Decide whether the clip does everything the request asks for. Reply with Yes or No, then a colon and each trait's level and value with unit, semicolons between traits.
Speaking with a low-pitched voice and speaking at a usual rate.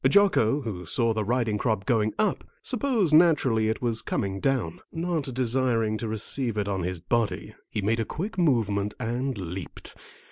Yes: low, 115 Hz; average, 170 wpm